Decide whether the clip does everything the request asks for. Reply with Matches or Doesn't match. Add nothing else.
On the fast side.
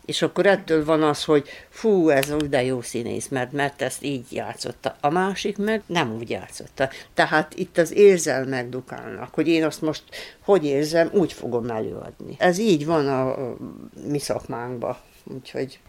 Matches